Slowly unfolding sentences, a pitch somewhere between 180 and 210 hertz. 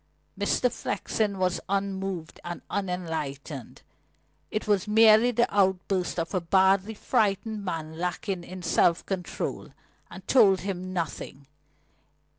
Yes: slow, 115 wpm; high, 190 Hz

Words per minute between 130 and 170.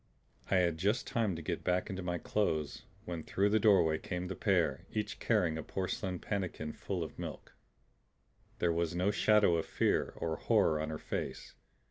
No: average, 180 wpm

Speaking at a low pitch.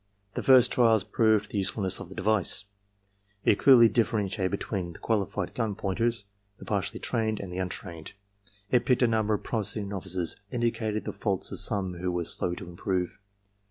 Yes: low, 105 Hz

